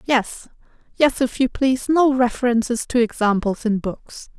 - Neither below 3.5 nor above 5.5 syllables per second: Yes, 4.6 syllables/s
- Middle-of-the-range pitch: No, high, 240 Hz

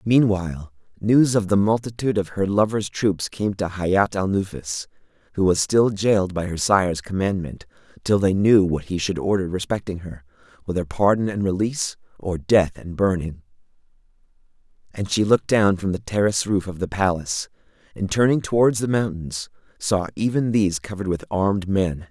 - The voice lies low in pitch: Yes, very low, 95 Hz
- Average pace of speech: Yes, average, 170 wpm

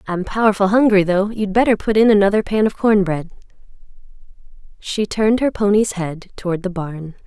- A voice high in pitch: Yes, high, 200 Hz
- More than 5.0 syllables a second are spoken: Yes, 5.4 syllables/s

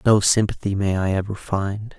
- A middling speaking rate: Yes, average, 180 wpm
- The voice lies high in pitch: No, low, 100 Hz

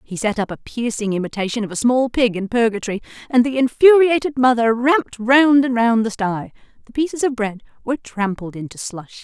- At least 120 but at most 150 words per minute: No, average, 195 wpm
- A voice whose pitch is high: Yes, high, 235 Hz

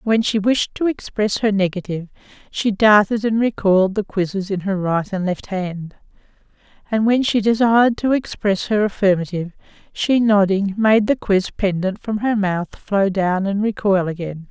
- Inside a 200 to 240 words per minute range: No, average, 170 wpm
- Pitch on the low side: No, high, 200 Hz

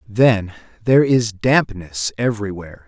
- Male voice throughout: Yes, male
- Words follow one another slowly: Yes, slow, 105 wpm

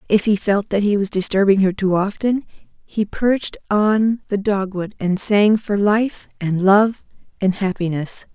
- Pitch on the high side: Yes, high, 200 Hz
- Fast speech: No, average, 165 wpm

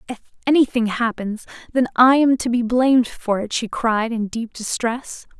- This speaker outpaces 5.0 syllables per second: No, 4.6 syllables/s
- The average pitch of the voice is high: Yes, high, 235 Hz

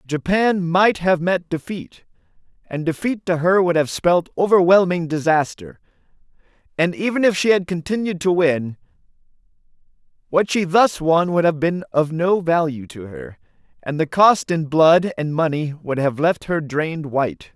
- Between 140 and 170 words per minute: Yes, average, 160 wpm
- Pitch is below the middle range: No, medium, 170 Hz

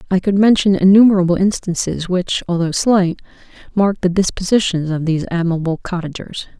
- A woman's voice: Yes, female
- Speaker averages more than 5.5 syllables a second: Yes, 5.7 syllables/s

